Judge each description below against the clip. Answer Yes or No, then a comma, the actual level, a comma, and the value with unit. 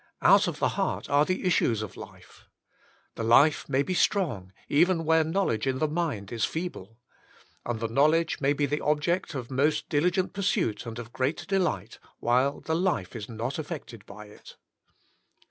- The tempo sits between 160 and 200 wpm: Yes, average, 175 wpm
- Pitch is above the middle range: No, medium, 145 Hz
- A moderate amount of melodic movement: No, wide, 6.0 semitones